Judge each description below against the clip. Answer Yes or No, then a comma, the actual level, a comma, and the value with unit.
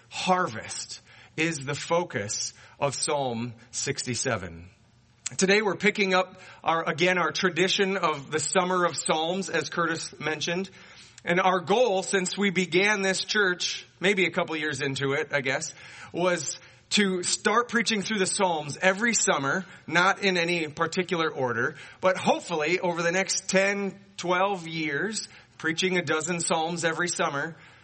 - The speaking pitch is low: No, medium, 175 Hz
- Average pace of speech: Yes, average, 145 wpm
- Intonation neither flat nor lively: Yes, average, 3.9 semitones